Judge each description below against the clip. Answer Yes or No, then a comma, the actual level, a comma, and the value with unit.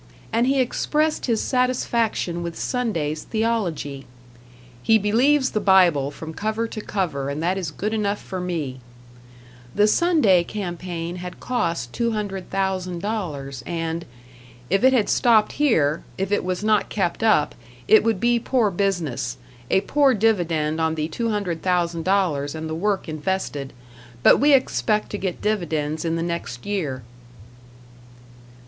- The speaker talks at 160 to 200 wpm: No, average, 140 wpm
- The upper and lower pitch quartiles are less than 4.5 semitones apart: No, average, 5.2 semitones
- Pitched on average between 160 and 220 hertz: Yes, high, 190 Hz